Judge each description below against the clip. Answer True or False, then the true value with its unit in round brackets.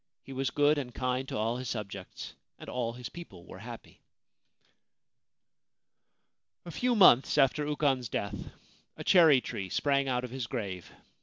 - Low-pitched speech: True (130 Hz)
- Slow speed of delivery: False (155 wpm)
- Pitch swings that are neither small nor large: True (3.9 semitones)